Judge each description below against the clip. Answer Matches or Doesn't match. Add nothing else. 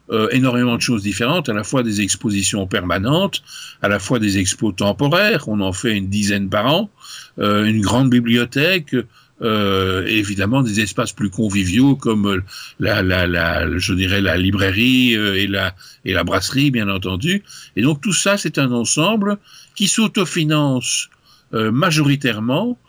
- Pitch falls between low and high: Doesn't match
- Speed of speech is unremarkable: Matches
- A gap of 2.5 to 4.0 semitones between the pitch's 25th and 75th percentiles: Doesn't match